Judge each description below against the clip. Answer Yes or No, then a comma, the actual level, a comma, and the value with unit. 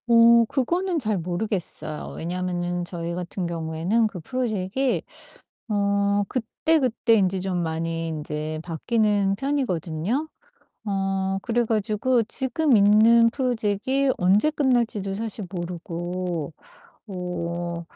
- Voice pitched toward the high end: Yes, high, 200 Hz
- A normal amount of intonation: Yes, average, 5.0 semitones